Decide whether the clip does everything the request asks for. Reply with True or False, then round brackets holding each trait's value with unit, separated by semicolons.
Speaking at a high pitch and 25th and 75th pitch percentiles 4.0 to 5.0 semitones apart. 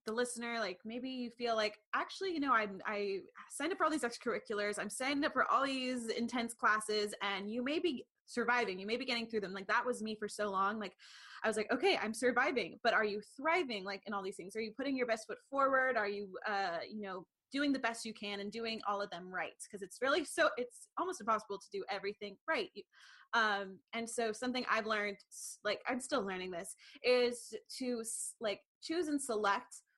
True (230 Hz; 4.3 semitones)